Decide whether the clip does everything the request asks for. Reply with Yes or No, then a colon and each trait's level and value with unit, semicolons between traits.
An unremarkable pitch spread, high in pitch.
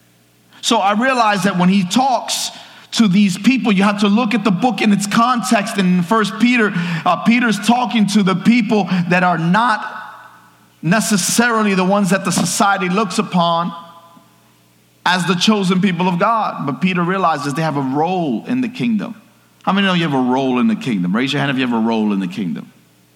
Yes: average, 4.6 semitones; high, 195 Hz